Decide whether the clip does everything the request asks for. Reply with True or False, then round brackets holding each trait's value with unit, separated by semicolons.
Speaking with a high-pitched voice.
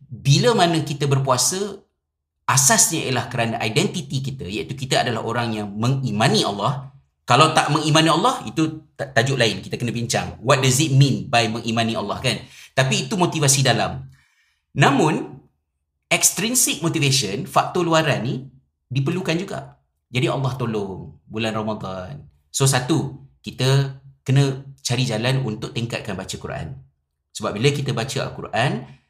False (135 Hz)